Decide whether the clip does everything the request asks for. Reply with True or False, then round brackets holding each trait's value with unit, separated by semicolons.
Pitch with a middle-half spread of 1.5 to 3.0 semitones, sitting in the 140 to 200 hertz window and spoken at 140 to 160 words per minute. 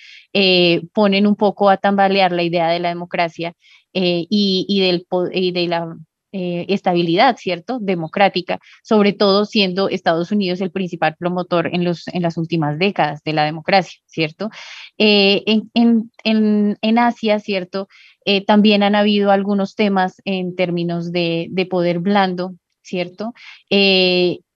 True (2.7 semitones; 185 Hz; 150 wpm)